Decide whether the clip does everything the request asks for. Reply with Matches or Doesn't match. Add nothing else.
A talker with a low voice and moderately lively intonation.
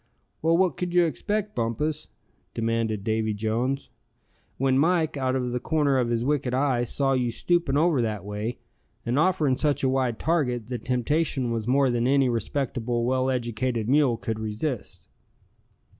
Matches